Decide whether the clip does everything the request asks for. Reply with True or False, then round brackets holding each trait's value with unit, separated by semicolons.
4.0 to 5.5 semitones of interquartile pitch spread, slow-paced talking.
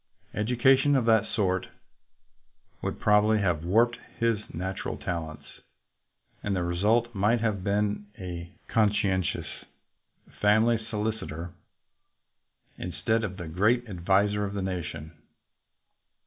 False (3.5 semitones; 110 wpm)